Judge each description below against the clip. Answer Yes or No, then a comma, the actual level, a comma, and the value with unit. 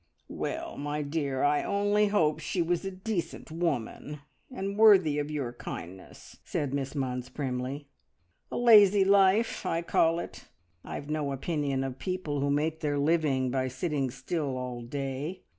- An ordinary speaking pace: Yes, average, 155 wpm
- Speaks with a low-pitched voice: No, medium, 150 Hz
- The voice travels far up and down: No, average, 4.7 semitones